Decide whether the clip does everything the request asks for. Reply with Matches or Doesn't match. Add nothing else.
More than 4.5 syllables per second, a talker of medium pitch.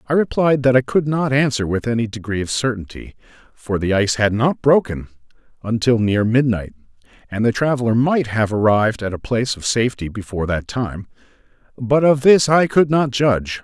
Doesn't match